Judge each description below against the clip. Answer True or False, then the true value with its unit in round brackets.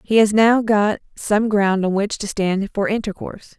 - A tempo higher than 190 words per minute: True (200 wpm)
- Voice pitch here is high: True (205 Hz)